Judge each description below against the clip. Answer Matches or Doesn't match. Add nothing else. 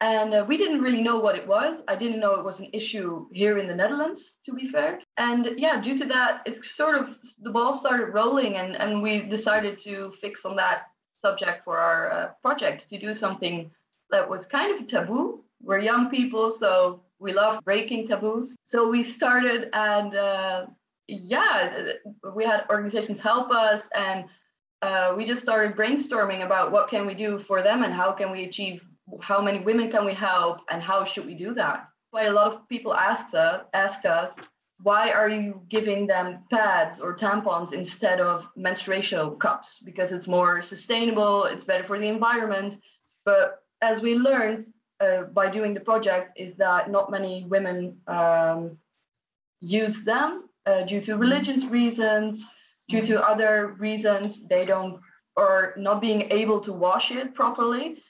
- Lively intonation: Doesn't match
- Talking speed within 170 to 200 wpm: Matches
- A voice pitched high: Matches